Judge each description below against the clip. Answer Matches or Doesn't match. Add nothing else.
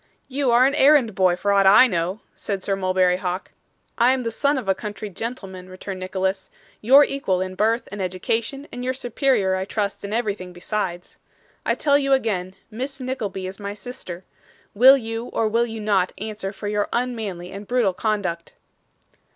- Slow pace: Doesn't match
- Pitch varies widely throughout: Doesn't match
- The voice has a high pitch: Matches